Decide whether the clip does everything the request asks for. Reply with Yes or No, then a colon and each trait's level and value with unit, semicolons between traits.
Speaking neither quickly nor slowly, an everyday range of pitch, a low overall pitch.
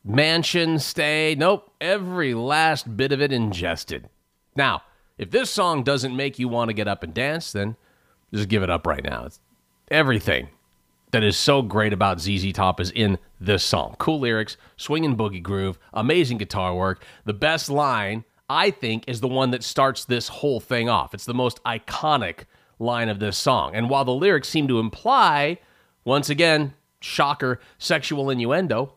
No: average, 175 wpm; wide, 6.0 semitones; low, 120 Hz